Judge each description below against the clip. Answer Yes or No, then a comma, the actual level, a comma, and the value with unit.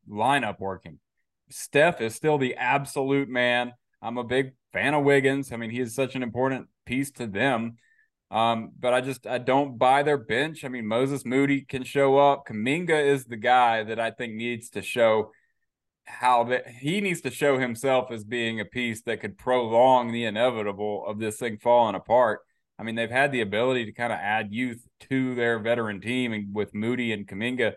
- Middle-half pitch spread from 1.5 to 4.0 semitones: Yes, average, 2.9 semitones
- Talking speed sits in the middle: Yes, average, 195 wpm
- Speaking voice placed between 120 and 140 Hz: Yes, low, 125 Hz